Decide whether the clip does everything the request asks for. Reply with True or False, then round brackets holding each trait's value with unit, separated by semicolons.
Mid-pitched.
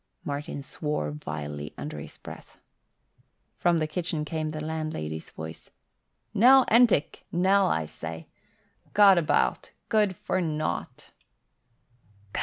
True (155 Hz)